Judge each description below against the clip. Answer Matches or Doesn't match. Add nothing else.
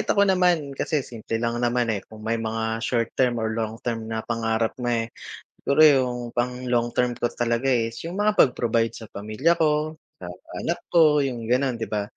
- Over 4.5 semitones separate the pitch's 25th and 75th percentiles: Doesn't match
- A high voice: Doesn't match